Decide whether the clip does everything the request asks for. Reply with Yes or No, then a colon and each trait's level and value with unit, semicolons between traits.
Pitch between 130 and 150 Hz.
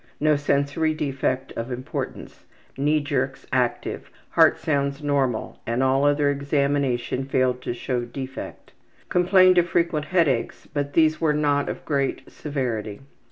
Yes: medium, 140 Hz